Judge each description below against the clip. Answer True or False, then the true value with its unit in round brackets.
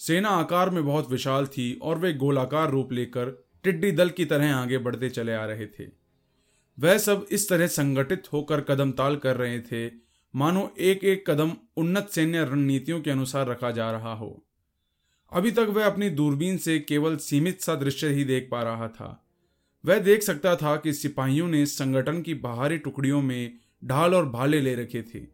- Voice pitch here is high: False (145 Hz)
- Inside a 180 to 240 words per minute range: True (185 wpm)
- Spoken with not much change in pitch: False (5.0 semitones)